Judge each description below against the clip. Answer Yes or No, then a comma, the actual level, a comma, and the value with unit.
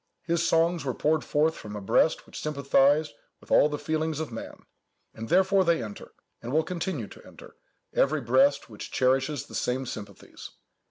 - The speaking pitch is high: No, medium, 145 Hz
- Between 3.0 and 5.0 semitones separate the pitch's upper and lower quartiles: Yes, average, 4.0 semitones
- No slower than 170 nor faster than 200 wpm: Yes, average, 175 wpm